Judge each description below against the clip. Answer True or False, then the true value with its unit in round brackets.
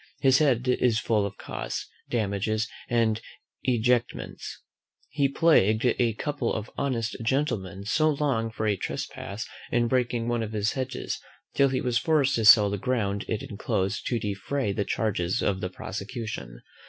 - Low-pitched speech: True (115 Hz)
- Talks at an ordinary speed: True (155 wpm)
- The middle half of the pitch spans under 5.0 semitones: True (3.7 semitones)